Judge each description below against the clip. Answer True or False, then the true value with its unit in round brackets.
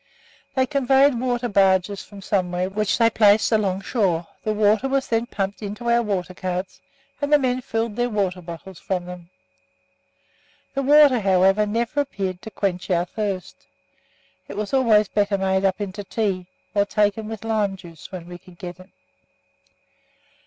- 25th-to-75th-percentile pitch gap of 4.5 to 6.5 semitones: False (3.5 semitones)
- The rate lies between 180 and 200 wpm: False (165 wpm)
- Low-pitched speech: False (205 Hz)